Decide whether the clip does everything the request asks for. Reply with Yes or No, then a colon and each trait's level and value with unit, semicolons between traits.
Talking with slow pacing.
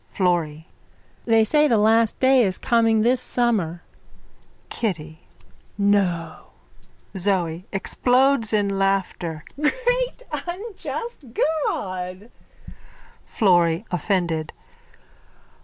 Yes: slow, 85 wpm